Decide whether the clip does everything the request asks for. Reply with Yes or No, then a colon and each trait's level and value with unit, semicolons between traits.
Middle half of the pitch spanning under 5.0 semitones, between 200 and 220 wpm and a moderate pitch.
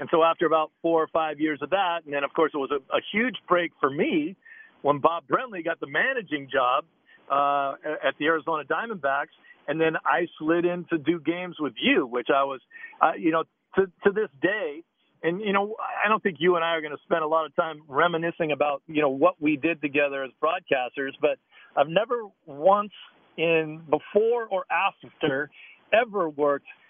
Yes: average, 4.0 semitones; fast, 205 wpm; medium, 165 Hz